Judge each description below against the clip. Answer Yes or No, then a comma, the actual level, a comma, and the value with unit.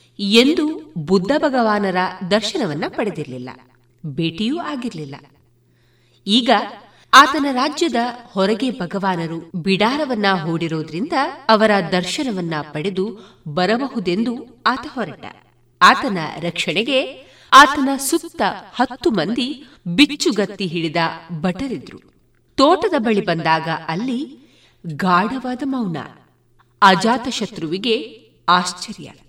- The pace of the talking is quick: No, average, 80 wpm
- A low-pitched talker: No, high, 200 Hz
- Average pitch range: No, wide, 7.2 semitones